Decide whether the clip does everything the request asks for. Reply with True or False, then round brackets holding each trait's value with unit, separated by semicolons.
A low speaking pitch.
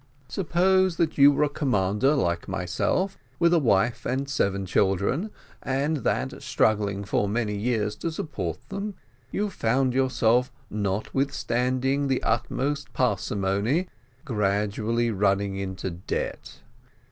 True (120 Hz)